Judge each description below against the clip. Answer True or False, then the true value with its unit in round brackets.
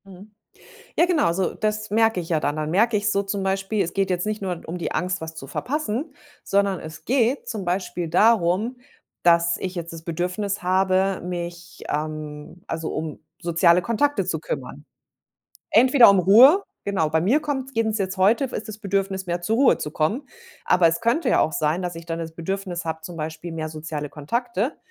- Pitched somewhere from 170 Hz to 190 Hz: True (185 Hz)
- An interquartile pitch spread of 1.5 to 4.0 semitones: False (4.4 semitones)